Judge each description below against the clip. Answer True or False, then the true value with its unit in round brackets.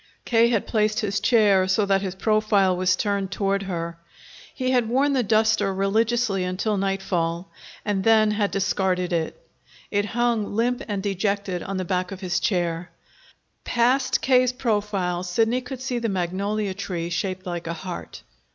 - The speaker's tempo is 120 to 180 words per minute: True (160 wpm)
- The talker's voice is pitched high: True (200 Hz)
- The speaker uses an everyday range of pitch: True (3.2 semitones)